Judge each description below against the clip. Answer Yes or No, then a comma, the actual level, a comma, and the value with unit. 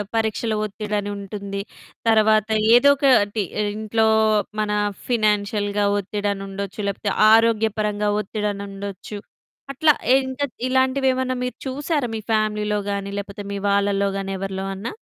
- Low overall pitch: No, high, 210 Hz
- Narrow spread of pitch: Yes, narrow, 2.1 semitones